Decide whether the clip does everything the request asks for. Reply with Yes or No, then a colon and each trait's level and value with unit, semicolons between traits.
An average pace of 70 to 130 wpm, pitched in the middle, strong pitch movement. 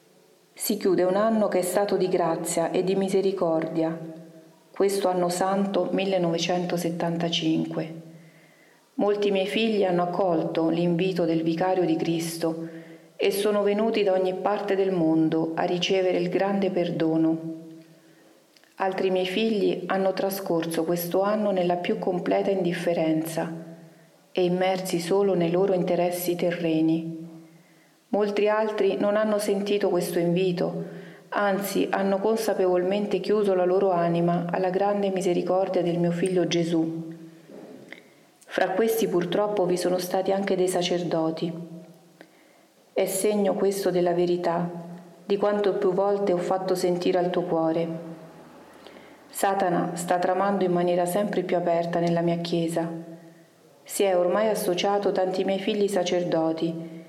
No: average, 125 wpm; medium, 180 Hz; narrow, 2.5 semitones